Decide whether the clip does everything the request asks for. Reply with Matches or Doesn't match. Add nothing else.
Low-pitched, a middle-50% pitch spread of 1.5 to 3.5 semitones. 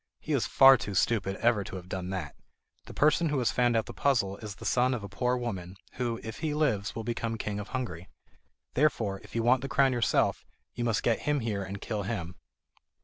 Doesn't match